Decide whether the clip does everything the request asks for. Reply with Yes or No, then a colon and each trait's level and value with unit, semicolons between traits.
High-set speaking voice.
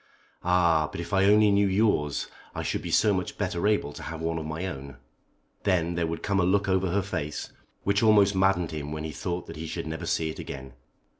No: very low, 85 Hz